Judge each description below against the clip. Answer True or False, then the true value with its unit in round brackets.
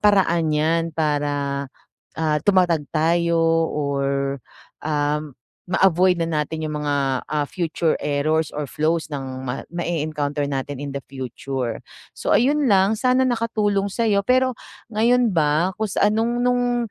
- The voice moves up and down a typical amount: False (5.7 semitones)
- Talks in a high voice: False (160 Hz)